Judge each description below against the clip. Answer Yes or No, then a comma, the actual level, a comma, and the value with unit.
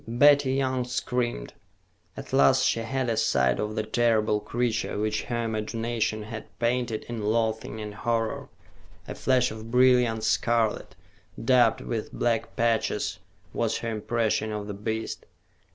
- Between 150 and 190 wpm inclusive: No, average, 140 wpm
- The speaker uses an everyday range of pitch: No, narrow, 1.9 semitones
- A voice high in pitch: No, low, 115 Hz